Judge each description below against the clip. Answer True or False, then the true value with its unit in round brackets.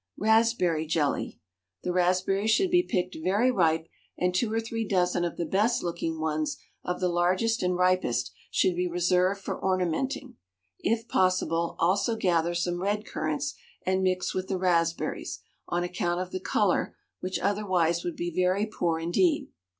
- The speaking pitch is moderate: True (180 Hz)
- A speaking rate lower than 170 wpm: True (160 wpm)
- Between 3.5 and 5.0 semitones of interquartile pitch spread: False (2.6 semitones)